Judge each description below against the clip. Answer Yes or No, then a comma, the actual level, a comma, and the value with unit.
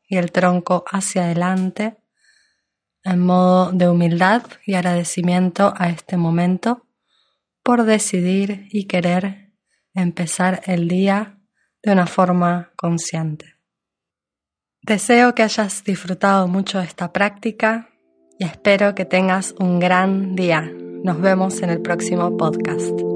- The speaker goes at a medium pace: No, slow, 120 wpm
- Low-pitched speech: No, medium, 185 Hz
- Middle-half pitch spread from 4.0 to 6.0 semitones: No, narrow, 2.4 semitones